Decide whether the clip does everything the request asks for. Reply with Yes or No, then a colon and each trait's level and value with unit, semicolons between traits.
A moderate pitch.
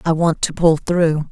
Yes: medium, 160 Hz